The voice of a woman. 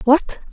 Yes: female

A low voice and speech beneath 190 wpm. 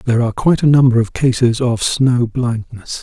No: low, 120 Hz; average, 200 wpm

